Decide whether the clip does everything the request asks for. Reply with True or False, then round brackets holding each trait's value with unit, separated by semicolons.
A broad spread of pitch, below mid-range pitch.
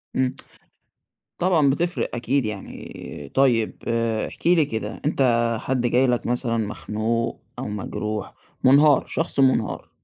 False (3.6 semitones; 120 Hz)